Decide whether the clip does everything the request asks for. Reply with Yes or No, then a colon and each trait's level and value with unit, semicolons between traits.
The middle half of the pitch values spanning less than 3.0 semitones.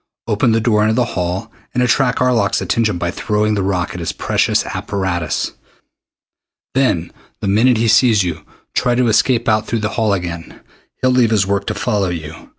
No: average, 4.2 semitones